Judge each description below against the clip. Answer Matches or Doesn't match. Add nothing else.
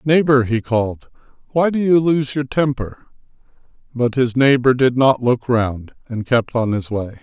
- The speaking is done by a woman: Doesn't match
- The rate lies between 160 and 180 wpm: Matches